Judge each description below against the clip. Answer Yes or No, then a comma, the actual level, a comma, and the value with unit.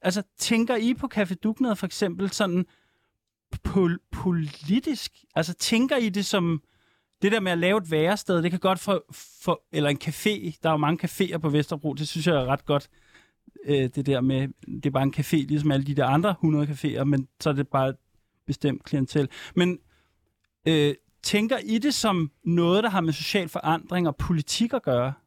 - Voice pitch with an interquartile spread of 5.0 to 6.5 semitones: Yes, wide, 5.4 semitones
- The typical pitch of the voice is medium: Yes, medium, 160 Hz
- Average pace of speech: Yes, average, 190 wpm